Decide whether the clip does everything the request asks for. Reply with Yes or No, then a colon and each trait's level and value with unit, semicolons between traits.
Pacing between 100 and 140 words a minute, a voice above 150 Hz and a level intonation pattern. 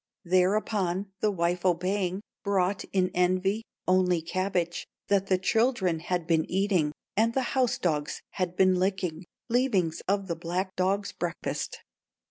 Yes: slow, 135 wpm; medium, 185 Hz; narrow, 2.1 semitones